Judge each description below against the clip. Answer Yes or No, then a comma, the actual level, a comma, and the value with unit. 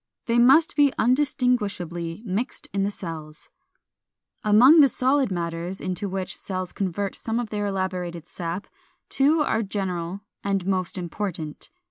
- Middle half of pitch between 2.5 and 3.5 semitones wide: No, average, 5.1 semitones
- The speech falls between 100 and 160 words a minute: Yes, average, 140 wpm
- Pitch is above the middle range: Yes, high, 195 Hz